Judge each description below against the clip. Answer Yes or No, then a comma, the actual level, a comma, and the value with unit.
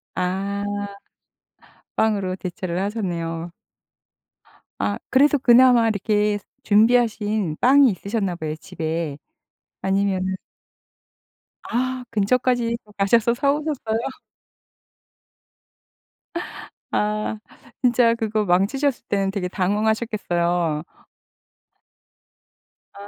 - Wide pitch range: No, average, 4.2 semitones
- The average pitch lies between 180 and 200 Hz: No, high, 210 Hz